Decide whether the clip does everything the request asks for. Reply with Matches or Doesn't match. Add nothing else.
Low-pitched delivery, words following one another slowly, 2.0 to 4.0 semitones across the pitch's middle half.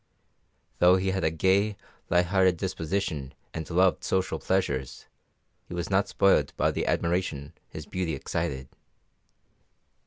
Matches